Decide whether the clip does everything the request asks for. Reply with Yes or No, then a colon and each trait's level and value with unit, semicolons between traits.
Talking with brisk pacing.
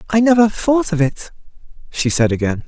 No: average, 180 wpm